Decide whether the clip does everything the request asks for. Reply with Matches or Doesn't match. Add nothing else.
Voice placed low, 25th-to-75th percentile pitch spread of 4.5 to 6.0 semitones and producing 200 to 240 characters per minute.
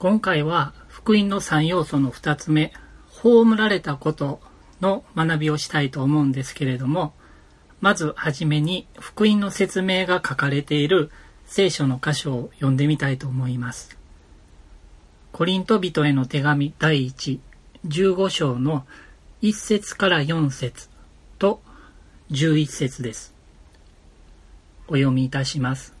Doesn't match